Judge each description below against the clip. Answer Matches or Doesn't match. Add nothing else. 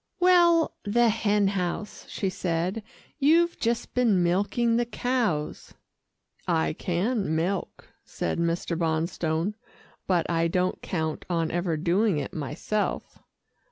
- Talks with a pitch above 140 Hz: Matches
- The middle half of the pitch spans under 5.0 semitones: Doesn't match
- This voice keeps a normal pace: Doesn't match